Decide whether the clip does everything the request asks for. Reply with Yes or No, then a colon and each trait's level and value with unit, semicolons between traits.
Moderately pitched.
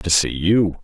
No: very low, 90 Hz